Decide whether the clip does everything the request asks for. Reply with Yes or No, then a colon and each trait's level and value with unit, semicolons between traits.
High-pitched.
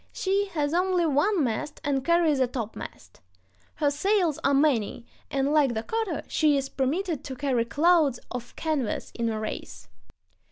Yes: very high, 285 Hz